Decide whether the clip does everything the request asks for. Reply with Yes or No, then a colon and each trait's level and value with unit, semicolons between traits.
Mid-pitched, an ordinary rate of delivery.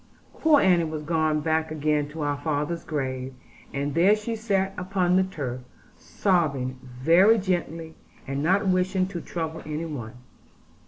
Yes: medium, 160 Hz; average, 150 wpm